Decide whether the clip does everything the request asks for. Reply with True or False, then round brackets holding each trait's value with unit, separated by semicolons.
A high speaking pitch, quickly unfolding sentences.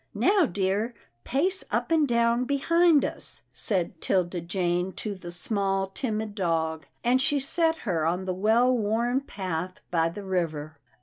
False (200 Hz; 160 wpm)